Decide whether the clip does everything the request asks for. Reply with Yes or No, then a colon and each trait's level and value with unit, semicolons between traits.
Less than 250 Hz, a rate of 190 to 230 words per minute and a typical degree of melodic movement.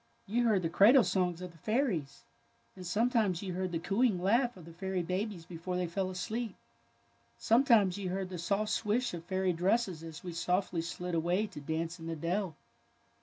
Yes: medium, 185 Hz; average, 200 wpm; average, 3.6 semitones